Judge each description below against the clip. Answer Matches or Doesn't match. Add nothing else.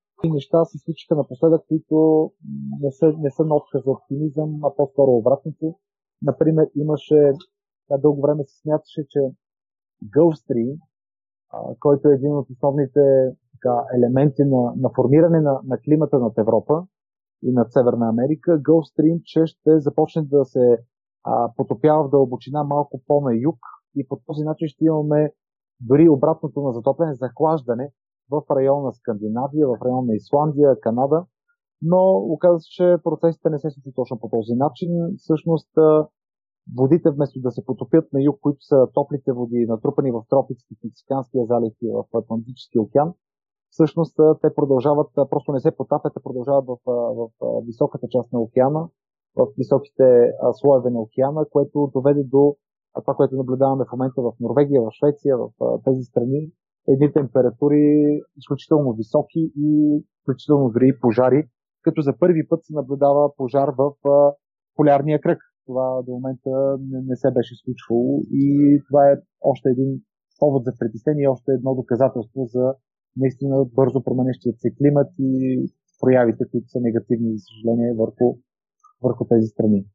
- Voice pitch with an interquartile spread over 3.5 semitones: Doesn't match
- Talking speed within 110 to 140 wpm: Doesn't match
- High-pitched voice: Doesn't match